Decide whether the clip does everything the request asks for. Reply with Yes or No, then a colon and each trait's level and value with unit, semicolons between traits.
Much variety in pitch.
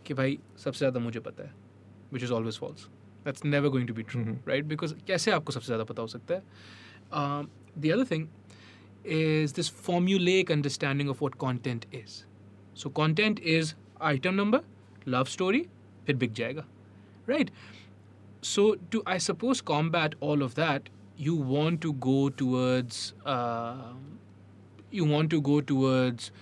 Yes: wide, 6.6 semitones